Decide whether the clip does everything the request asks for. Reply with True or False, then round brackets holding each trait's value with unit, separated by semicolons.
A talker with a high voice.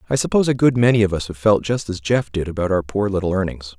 False (100 Hz)